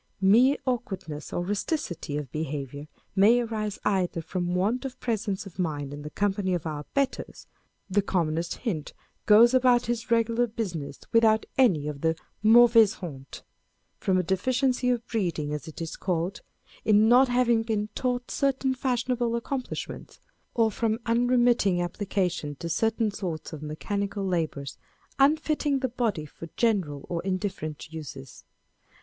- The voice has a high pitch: Yes, high, 205 Hz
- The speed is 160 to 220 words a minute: No, average, 150 wpm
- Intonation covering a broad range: Yes, wide, 6.4 semitones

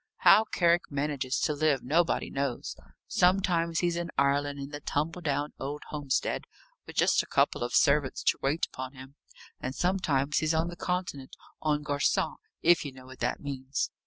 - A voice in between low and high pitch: Yes, medium, 145 Hz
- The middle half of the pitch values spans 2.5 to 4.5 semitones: Yes, average, 3.4 semitones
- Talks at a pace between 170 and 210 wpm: Yes, average, 175 wpm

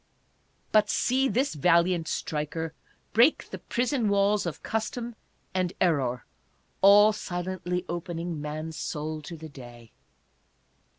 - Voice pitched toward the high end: No, medium, 175 Hz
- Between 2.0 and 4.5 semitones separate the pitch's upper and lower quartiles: No, average, 5.0 semitones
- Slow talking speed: Yes, slow, 115 wpm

